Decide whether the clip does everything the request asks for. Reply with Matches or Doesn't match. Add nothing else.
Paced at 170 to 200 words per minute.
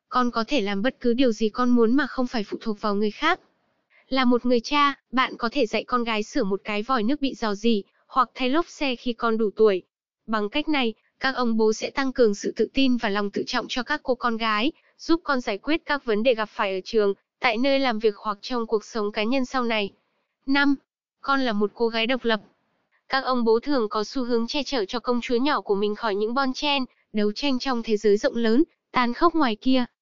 Doesn't match